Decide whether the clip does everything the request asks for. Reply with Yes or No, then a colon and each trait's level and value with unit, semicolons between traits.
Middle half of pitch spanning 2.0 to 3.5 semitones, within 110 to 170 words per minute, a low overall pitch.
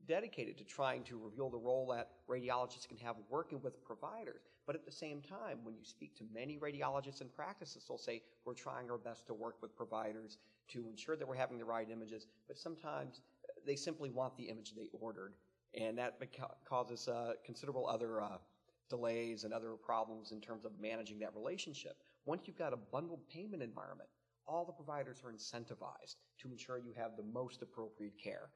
No: average, 2.9 semitones; average, 195 wpm; low, 120 Hz